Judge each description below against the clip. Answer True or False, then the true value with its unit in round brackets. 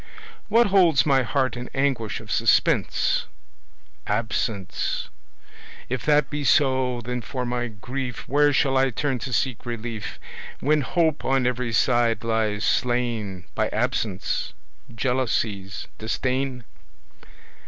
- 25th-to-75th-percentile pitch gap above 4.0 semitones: False (2.9 semitones)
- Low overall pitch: True (125 Hz)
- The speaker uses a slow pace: True (120 wpm)